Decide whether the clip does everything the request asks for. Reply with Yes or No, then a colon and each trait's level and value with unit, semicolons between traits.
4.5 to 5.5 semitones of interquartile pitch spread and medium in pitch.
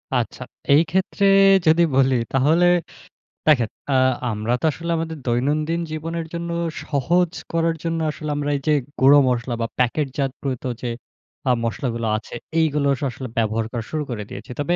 Yes: average, 4.8 semitones; medium, 145 Hz